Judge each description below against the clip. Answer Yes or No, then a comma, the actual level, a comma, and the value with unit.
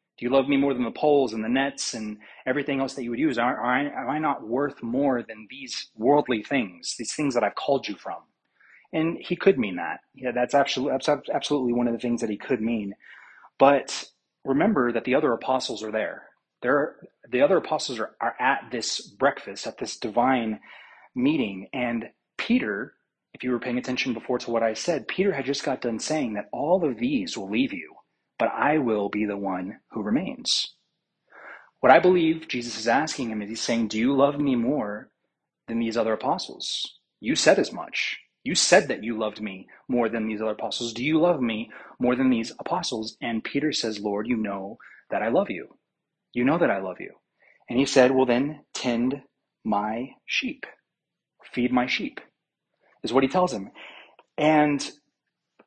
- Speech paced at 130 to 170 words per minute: No, average, 195 wpm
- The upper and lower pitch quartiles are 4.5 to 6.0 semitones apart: No, average, 3.8 semitones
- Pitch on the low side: Yes, low, 125 Hz